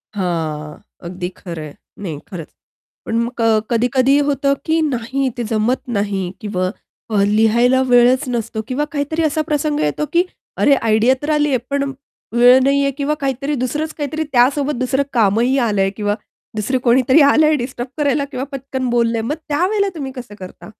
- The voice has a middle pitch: No, very high, 255 Hz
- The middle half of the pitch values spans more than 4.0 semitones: Yes, average, 4.5 semitones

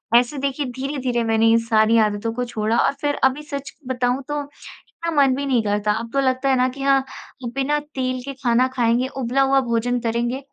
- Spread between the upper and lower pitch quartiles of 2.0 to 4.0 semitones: Yes, average, 2.8 semitones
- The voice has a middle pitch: No, very high, 255 Hz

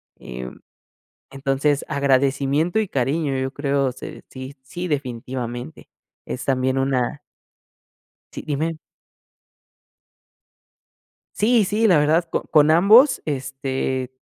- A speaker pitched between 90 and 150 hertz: Yes, medium, 140 Hz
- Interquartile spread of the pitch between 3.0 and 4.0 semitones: Yes, average, 3.3 semitones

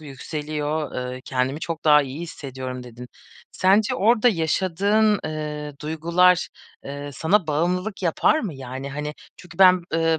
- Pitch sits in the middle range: Yes, medium, 155 Hz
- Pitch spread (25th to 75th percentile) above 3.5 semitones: Yes, average, 4.1 semitones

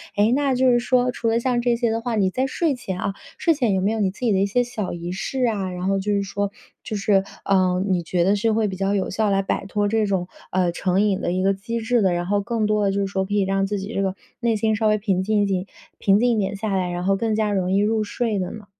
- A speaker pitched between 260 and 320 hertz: No, high, 205 Hz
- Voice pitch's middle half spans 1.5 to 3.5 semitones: Yes, average, 2.7 semitones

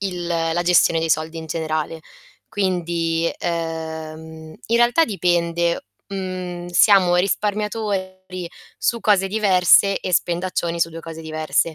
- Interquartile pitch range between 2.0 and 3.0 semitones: Yes, narrow, 2.4 semitones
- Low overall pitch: No, medium, 175 Hz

